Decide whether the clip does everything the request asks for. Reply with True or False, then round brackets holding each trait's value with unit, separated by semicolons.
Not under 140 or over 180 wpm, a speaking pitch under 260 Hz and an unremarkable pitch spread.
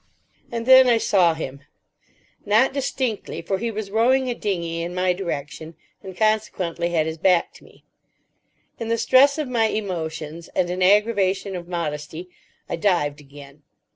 True (160 wpm; 185 Hz; 5.0 semitones)